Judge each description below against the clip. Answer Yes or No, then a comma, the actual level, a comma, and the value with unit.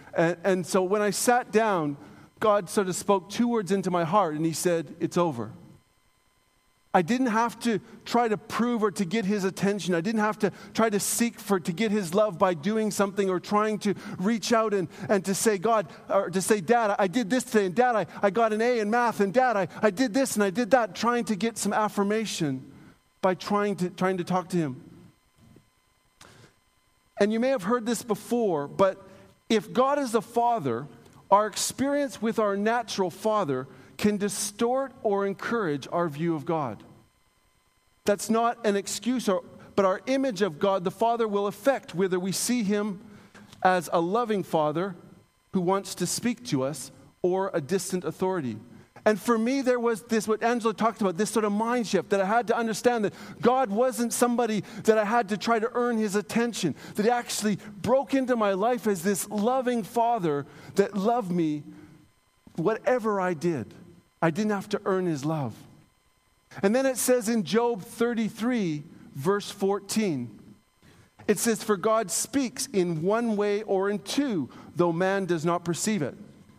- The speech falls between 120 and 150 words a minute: No, average, 185 wpm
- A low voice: No, high, 205 Hz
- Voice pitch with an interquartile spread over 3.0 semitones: Yes, average, 3.8 semitones